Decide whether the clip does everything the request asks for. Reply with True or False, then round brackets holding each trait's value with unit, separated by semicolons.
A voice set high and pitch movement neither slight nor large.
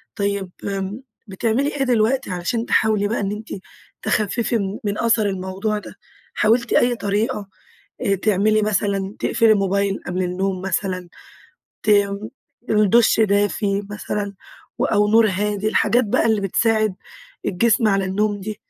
False (205 Hz; 2.0 semitones)